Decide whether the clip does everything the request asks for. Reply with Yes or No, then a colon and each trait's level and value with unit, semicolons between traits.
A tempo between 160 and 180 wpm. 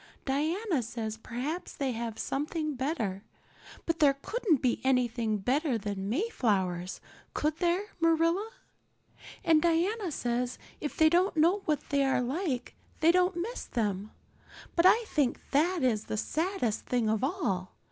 No: average, 145 wpm